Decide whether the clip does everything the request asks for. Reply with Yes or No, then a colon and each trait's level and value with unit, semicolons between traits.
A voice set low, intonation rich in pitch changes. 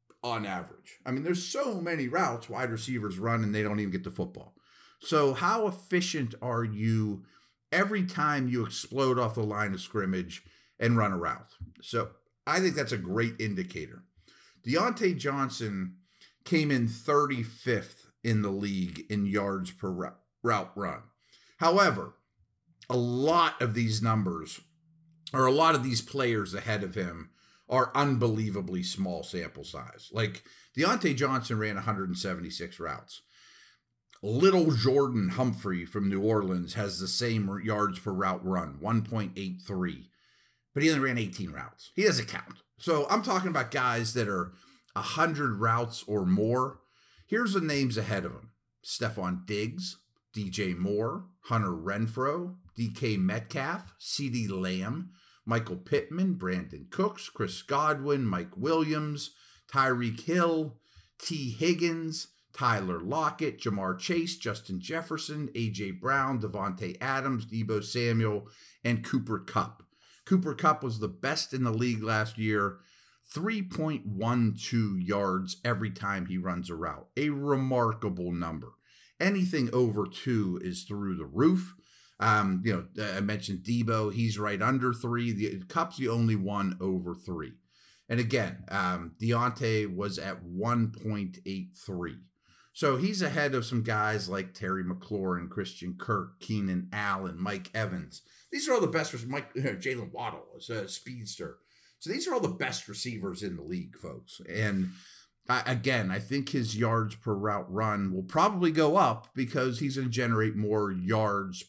Yes: low, 115 Hz; wide, 5.9 semitones